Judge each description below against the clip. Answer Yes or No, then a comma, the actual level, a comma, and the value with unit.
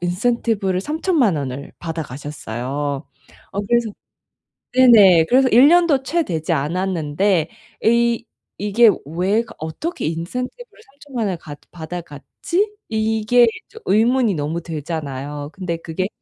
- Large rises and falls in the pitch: Yes, wide, 7.1 semitones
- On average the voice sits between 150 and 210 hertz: Yes, high, 190 Hz